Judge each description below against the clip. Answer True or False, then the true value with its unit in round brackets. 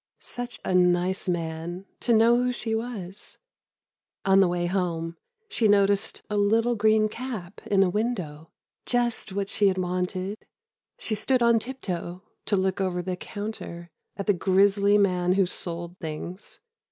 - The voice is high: True (195 Hz)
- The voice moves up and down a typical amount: True (3.4 semitones)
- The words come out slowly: False (150 wpm)